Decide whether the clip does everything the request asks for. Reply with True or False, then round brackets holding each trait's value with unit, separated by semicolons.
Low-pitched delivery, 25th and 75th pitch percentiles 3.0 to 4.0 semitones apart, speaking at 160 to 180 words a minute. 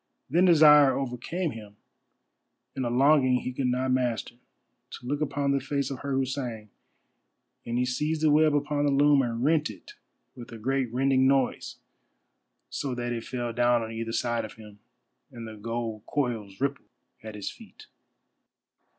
True (130 Hz; 3.3 semitones; 170 wpm)